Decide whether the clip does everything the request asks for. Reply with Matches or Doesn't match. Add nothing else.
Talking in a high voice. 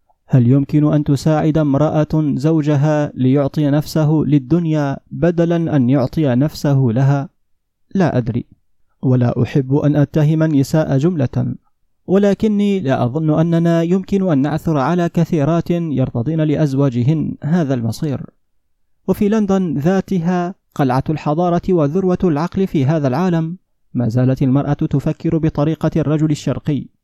Doesn't match